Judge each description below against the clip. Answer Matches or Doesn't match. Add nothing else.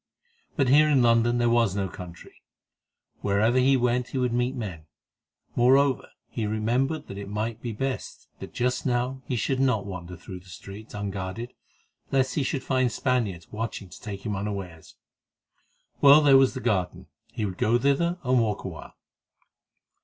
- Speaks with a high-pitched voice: Doesn't match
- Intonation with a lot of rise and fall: Doesn't match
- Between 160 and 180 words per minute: Matches